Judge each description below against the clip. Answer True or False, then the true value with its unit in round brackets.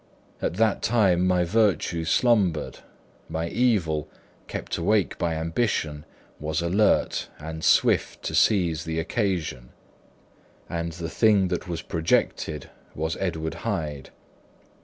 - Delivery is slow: True (115 wpm)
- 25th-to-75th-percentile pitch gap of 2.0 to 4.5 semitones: True (3.5 semitones)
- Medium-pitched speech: False (85 Hz)